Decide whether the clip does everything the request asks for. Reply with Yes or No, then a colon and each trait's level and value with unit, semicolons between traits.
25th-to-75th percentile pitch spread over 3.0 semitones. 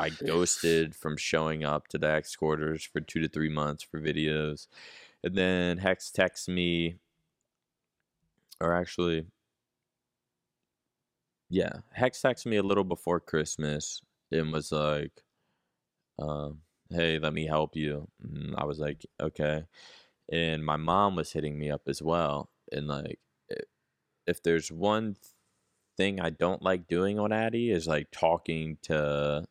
No: average, 2.7 semitones